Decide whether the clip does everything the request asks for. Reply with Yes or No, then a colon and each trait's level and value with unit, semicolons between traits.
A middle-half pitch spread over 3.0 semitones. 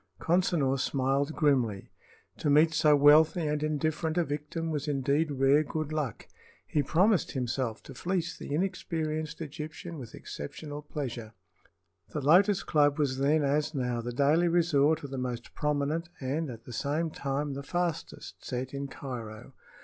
No: average, 2.7 semitones